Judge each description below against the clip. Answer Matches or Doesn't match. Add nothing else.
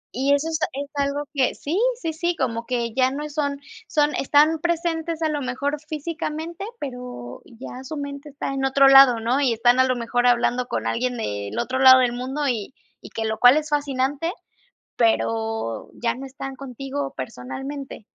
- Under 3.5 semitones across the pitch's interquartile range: Matches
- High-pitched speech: Matches